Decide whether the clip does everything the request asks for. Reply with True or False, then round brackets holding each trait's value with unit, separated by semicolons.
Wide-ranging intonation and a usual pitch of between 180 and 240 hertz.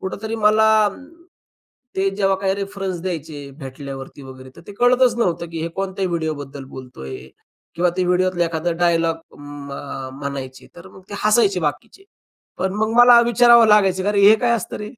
True (6.1 semitones; 185 Hz)